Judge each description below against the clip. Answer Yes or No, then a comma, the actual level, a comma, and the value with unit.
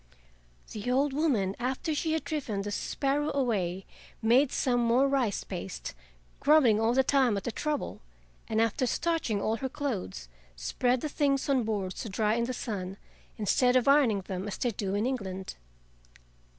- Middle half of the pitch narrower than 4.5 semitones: No, average, 5.1 semitones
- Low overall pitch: No, high, 240 Hz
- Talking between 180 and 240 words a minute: No, average, 170 wpm